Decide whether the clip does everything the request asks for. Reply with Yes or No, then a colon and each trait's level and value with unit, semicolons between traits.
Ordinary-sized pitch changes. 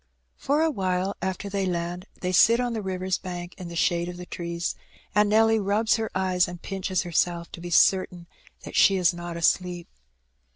No: narrow, 2.3 semitones